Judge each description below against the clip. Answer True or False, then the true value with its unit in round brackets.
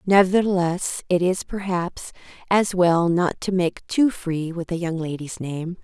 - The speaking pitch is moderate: True (180 Hz)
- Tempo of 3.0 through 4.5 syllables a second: True (4.1 syllables/s)